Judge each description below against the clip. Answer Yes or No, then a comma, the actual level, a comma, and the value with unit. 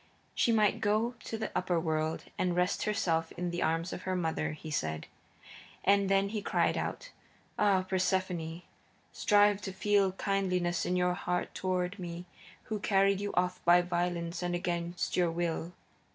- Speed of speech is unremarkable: Yes, average, 160 wpm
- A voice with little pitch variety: Yes, narrow, 2.3 semitones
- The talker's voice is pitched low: No, medium, 180 Hz